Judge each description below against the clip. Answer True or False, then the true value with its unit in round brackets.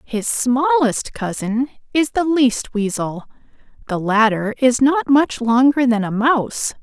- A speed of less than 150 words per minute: True (140 wpm)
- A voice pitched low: False (245 Hz)